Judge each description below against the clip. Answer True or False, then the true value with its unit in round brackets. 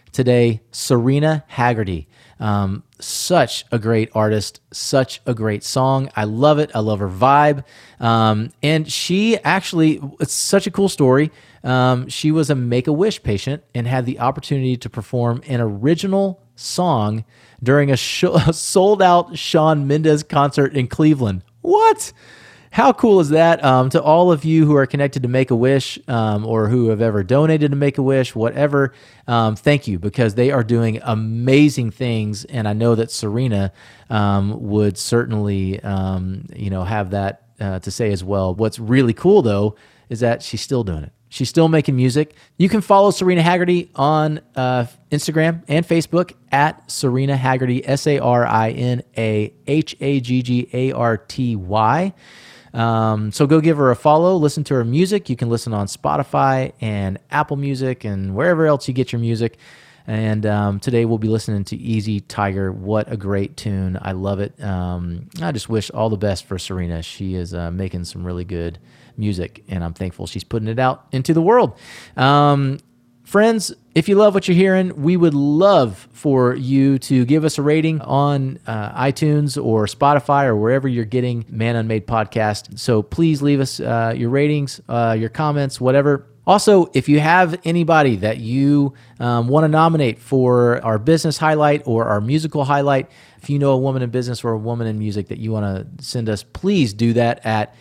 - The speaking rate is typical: True (185 wpm)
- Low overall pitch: True (125 Hz)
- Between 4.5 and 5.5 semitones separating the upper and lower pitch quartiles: True (5.1 semitones)